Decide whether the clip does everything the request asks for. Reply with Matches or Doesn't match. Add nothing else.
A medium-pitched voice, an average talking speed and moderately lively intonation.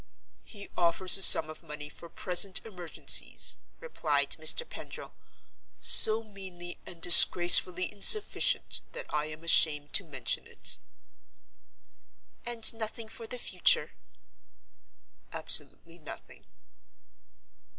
Doesn't match